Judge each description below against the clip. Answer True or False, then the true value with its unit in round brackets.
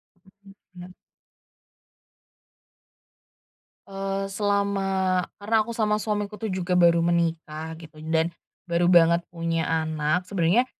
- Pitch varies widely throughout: False (3.2 semitones)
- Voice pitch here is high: False (180 Hz)